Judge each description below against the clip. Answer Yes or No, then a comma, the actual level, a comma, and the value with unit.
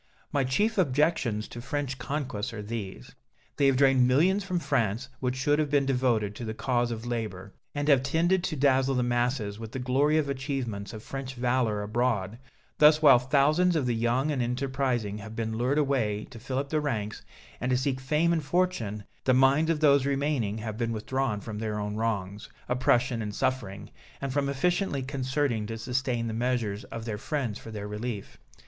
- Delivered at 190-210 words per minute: Yes, average, 195 wpm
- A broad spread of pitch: No, average, 3.9 semitones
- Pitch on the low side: Yes, low, 125 Hz